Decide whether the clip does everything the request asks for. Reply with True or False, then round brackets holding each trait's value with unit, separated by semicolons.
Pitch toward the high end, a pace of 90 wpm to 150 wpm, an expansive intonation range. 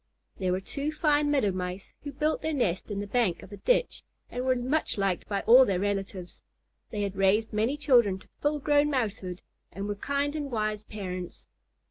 False (215 Hz; 195 wpm; 6.4 semitones)